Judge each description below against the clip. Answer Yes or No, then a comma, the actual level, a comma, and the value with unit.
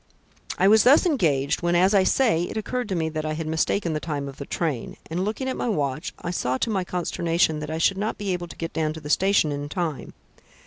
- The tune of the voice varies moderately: Yes, average, 4.3 semitones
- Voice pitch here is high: No, medium, 170 Hz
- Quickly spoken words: Yes, fast, 255 wpm